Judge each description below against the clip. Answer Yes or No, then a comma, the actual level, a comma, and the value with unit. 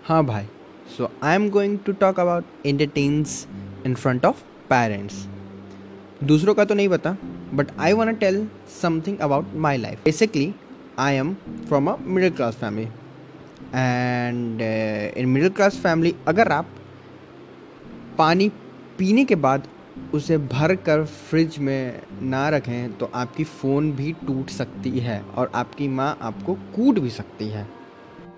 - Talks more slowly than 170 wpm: Yes, average, 145 wpm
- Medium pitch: Yes, medium, 145 Hz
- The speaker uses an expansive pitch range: Yes, wide, 6.2 semitones